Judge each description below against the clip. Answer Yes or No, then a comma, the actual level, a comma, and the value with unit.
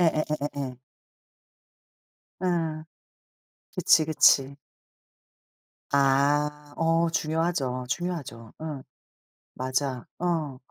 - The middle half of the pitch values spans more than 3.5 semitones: No, average, 3.2 semitones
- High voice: No, medium, 150 Hz